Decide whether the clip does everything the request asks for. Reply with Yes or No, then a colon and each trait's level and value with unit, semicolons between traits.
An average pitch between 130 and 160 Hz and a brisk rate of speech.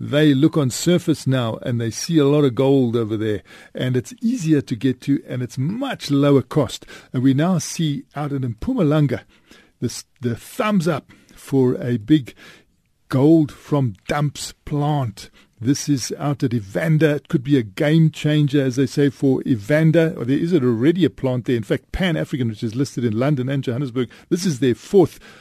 No: medium, 140 Hz; average, 190 wpm